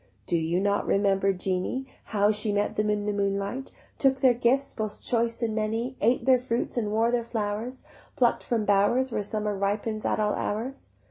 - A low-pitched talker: No, high, 215 Hz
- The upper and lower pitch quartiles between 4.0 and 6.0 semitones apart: No, average, 2.8 semitones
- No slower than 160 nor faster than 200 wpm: Yes, average, 190 wpm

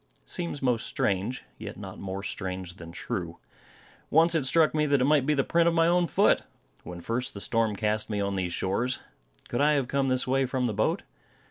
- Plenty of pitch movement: Yes, wide, 6.7 semitones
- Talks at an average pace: No, fast, 220 wpm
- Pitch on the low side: Yes, low, 125 Hz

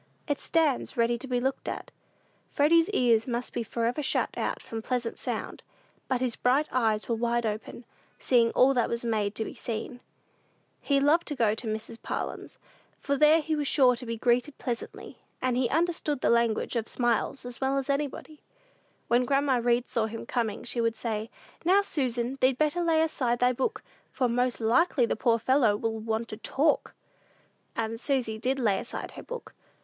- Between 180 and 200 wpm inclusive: Yes, average, 190 wpm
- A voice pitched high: Yes, high, 245 Hz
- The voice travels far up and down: No, average, 3.2 semitones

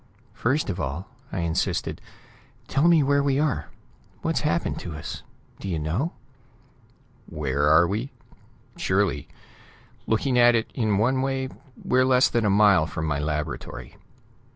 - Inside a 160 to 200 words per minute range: No, average, 145 wpm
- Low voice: Yes, low, 105 Hz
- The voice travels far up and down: Yes, wide, 8.7 semitones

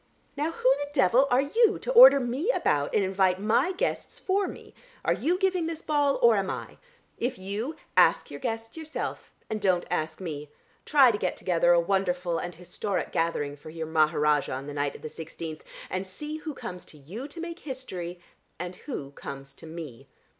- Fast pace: No, average, 195 wpm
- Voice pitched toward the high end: Yes, high, 195 Hz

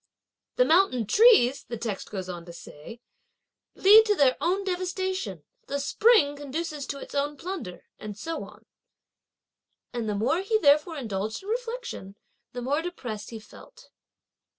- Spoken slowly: No, average, 150 wpm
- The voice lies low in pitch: No, very high, 285 Hz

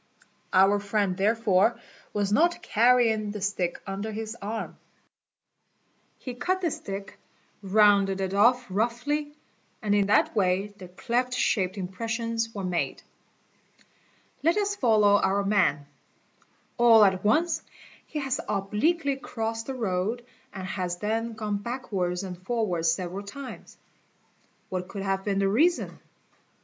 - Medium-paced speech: No, slow, 130 wpm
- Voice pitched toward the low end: No, high, 210 Hz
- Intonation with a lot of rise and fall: No, average, 3.6 semitones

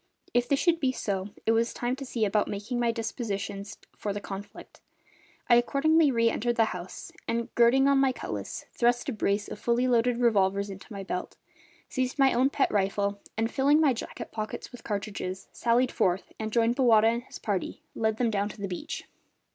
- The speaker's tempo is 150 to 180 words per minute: No, average, 195 wpm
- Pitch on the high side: Yes, high, 230 Hz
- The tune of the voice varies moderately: Yes, average, 3.5 semitones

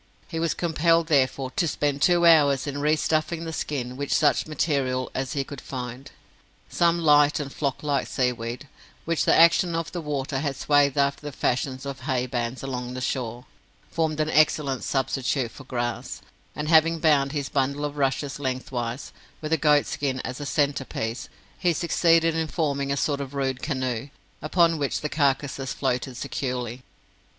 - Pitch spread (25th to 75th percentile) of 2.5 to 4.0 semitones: Yes, average, 3.0 semitones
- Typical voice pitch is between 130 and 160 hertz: Yes, medium, 140 Hz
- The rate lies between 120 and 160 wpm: No, average, 175 wpm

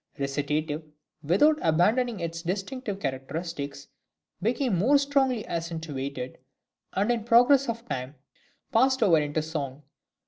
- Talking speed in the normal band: No, slow, 110 wpm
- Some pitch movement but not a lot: No, wide, 8.2 semitones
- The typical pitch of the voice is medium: Yes, medium, 170 Hz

